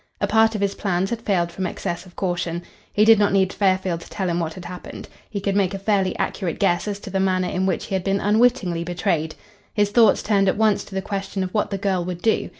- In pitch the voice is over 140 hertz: Yes, high, 190 Hz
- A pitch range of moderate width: No, narrow, 2.3 semitones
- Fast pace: Yes, fast, 255 wpm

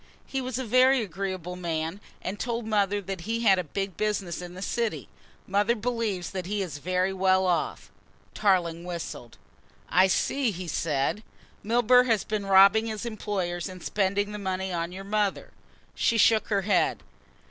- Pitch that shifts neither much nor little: Yes, average, 3.0 semitones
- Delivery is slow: No, average, 170 wpm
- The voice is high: Yes, high, 195 Hz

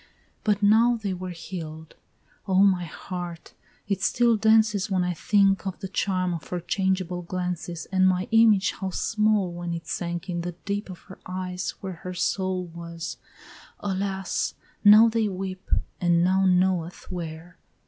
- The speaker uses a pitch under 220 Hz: Yes, medium, 185 Hz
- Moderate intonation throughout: No, narrow, 2.2 semitones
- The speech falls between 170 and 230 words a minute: No, average, 160 wpm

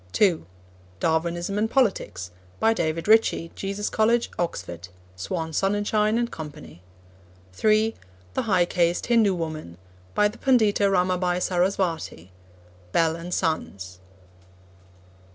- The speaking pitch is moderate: Yes, medium, 180 Hz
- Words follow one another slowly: Yes, slow, 110 wpm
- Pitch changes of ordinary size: Yes, average, 4.6 semitones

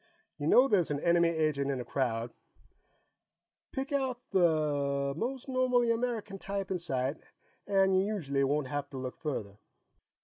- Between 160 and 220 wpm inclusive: No, average, 150 wpm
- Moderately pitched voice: Yes, medium, 165 Hz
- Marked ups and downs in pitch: Yes, wide, 7.0 semitones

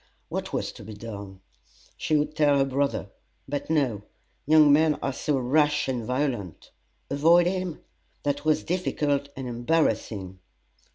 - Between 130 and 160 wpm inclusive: Yes, average, 145 wpm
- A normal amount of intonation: Yes, average, 4.0 semitones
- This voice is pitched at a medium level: Yes, medium, 145 Hz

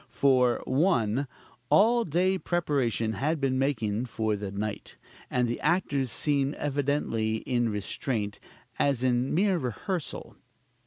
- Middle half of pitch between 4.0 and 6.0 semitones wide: Yes, average, 4.7 semitones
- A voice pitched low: Yes, low, 130 Hz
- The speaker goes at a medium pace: No, slow, 125 wpm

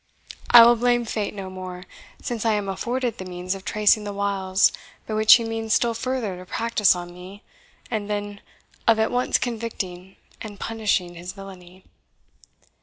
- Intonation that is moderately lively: Yes, average, 3.3 semitones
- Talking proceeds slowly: No, average, 170 wpm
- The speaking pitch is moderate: No, high, 205 Hz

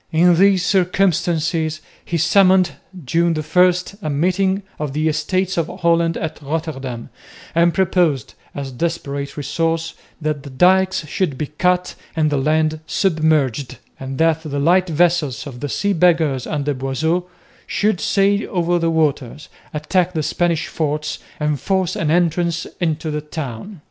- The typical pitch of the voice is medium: Yes, medium, 160 Hz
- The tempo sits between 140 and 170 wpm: Yes, average, 150 wpm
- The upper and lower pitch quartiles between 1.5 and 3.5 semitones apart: Yes, average, 3.0 semitones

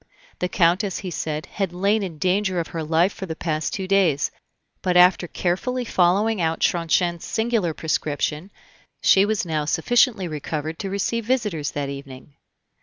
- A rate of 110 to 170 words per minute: Yes, average, 160 wpm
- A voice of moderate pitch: Yes, medium, 180 Hz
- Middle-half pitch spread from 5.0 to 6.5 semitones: No, average, 3.8 semitones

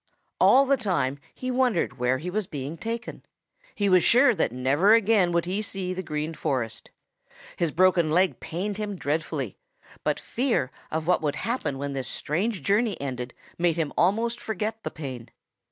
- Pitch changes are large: Yes, wide, 6.6 semitones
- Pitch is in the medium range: Yes, medium, 180 Hz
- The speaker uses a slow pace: No, average, 170 wpm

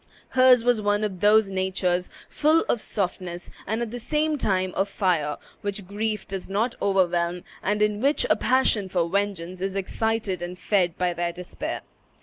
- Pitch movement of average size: Yes, average, 3.3 semitones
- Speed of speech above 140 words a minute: Yes, average, 170 wpm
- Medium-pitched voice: No, high, 195 Hz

